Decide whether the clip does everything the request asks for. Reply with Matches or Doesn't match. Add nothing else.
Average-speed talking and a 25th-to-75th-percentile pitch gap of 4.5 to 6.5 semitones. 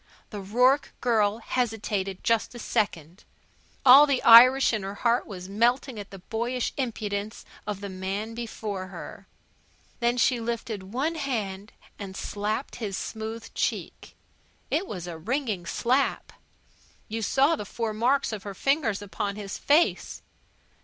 Doesn't match